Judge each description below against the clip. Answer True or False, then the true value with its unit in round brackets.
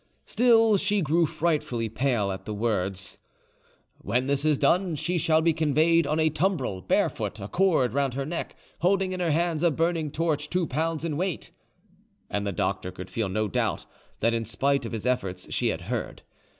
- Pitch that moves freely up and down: True (6.7 semitones)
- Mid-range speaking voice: True (150 Hz)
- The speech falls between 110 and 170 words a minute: False (190 wpm)